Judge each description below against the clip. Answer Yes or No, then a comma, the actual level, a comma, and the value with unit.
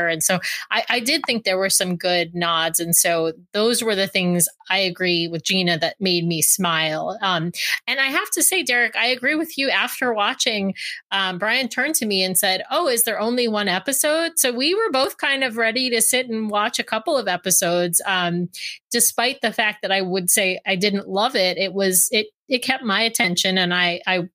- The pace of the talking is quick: Yes, fast, 215 wpm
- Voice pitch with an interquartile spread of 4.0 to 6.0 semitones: Yes, average, 5.0 semitones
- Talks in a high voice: Yes, high, 195 Hz